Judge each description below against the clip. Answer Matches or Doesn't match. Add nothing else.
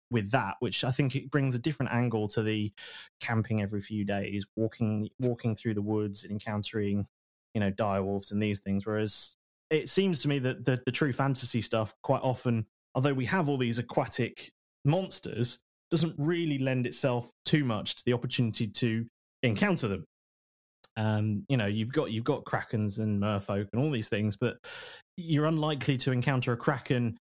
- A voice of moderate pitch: Doesn't match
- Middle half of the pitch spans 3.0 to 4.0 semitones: Doesn't match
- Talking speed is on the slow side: Doesn't match